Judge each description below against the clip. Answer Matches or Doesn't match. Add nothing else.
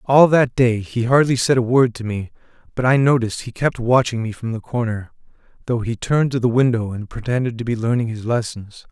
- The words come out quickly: Matches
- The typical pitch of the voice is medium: Doesn't match